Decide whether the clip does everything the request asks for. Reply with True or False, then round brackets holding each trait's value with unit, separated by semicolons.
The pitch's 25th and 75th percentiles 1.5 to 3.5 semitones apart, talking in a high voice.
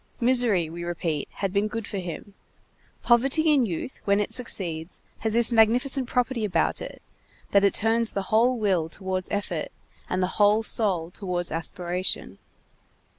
False (4.5 semitones; 205 Hz)